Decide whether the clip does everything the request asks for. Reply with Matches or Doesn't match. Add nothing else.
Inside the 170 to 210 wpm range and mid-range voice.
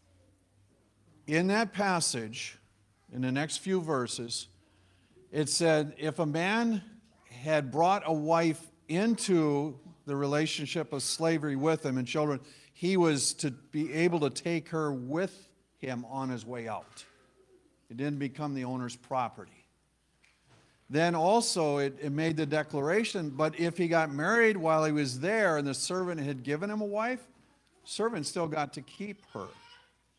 Doesn't match